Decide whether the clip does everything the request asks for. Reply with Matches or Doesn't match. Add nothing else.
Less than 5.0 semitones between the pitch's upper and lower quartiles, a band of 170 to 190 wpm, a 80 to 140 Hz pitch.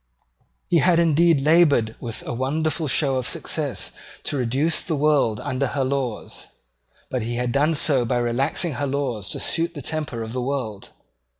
Matches